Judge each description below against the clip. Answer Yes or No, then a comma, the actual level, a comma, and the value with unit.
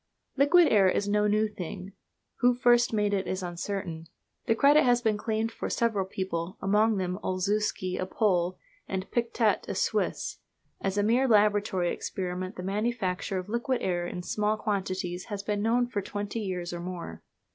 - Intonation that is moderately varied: Yes, average, 3.1 semitones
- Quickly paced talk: No, average, 170 wpm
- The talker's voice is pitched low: No, high, 205 Hz